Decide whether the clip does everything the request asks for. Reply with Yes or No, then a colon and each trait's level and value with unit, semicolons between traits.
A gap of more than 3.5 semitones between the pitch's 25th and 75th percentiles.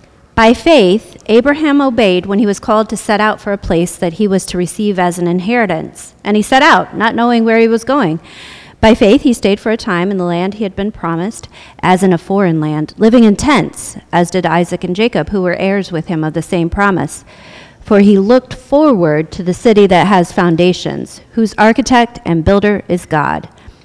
Yes: average, 4.1 semitones